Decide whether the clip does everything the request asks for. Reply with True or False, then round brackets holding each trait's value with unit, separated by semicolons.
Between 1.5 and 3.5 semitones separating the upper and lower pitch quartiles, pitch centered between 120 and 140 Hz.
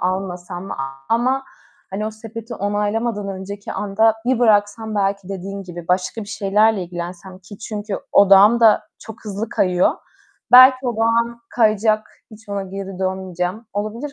False (2.8 semitones; 205 Hz)